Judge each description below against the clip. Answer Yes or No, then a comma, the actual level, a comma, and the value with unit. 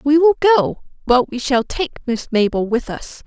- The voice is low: No, very high, 265 Hz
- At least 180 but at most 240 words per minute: Yes, average, 200 wpm